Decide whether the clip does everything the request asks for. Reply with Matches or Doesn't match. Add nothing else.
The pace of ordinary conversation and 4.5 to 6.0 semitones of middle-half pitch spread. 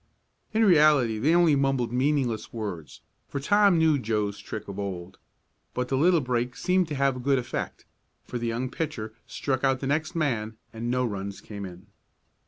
Matches